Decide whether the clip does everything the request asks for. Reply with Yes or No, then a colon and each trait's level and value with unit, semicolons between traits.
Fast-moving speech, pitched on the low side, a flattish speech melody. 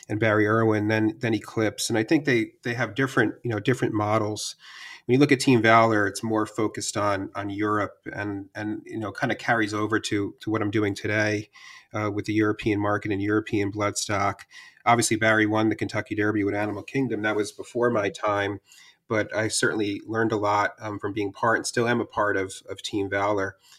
Yes: fast, 210 wpm; low, 105 Hz; narrow, 1.5 semitones